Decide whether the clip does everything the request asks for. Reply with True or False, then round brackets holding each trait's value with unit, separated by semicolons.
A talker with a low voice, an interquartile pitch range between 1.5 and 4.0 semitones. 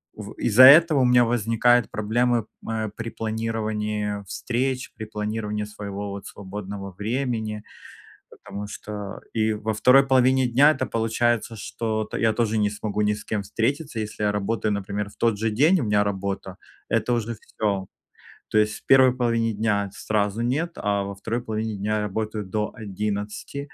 True (110 Hz; 2.4 semitones)